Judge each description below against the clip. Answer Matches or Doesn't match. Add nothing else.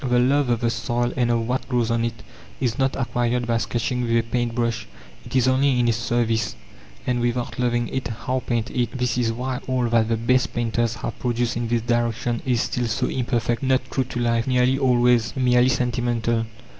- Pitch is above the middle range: Doesn't match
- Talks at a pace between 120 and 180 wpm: Doesn't match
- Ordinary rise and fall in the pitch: Doesn't match